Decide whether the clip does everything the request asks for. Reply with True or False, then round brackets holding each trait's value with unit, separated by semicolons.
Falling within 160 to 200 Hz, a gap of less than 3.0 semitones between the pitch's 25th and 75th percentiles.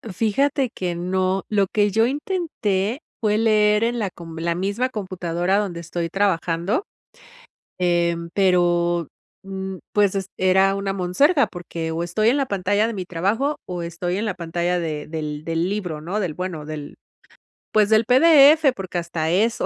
False (190 Hz; 3.8 semitones)